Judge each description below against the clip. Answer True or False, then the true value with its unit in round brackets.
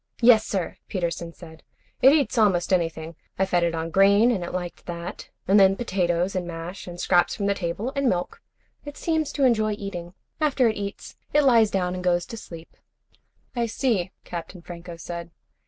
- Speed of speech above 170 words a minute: True (190 wpm)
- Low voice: False (185 Hz)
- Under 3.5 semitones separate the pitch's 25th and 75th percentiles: False (4.2 semitones)